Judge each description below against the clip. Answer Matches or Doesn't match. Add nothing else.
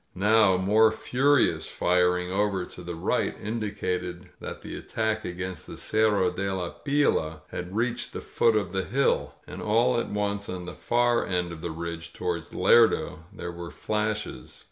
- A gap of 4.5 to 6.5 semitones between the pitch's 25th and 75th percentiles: Doesn't match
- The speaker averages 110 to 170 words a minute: Matches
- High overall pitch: Doesn't match